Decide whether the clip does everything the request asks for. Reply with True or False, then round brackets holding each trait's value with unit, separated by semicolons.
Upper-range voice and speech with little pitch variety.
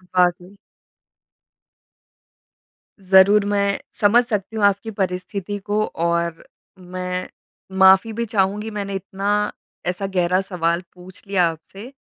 True (195 Hz; 2.1 semitones)